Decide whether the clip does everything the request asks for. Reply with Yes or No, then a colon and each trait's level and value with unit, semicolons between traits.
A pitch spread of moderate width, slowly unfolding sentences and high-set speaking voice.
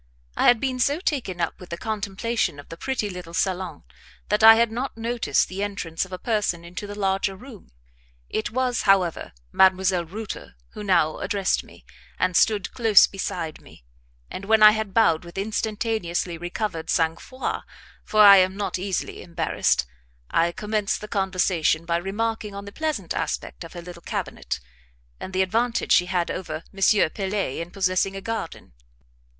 No: average, 3.7 semitones; average, 170 wpm; high, 195 Hz